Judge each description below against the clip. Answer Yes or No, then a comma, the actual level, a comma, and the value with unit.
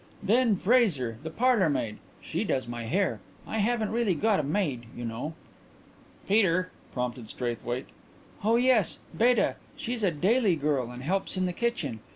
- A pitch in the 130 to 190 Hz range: Yes, medium, 185 Hz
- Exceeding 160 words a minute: No, average, 155 wpm